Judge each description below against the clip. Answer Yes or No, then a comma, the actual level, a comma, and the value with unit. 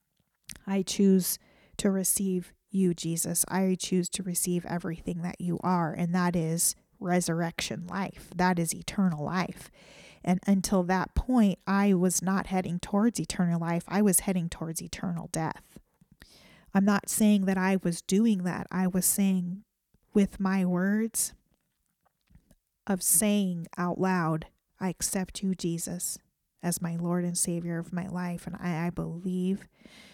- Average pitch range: No, narrow, 1.9 semitones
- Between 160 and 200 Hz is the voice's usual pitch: Yes, medium, 185 Hz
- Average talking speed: Yes, average, 145 wpm